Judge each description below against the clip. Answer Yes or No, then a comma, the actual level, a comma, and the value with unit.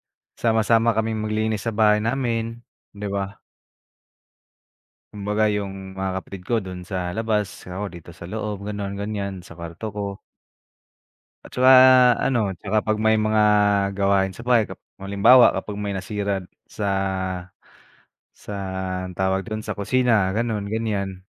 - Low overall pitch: Yes, low, 105 Hz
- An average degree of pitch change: No, narrow, 2.2 semitones